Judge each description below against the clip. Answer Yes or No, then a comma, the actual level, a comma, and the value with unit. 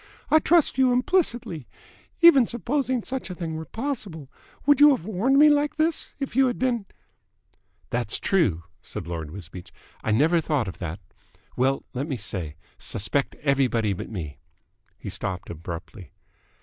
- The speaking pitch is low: No, medium, 160 Hz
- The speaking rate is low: No, average, 160 wpm